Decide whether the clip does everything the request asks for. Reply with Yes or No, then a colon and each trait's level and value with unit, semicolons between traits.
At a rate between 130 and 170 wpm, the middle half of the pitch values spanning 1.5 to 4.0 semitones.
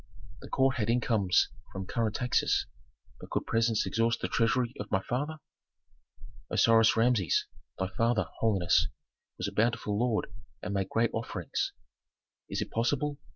Yes: average, 145 wpm; narrow, 2.6 semitones